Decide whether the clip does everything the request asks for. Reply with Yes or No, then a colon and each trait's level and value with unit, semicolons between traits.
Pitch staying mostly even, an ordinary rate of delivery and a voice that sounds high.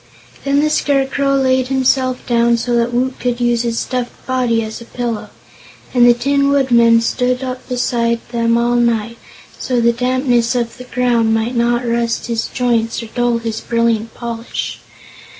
Yes: narrow, 1.6 semitones; average, 170 wpm; high, 240 Hz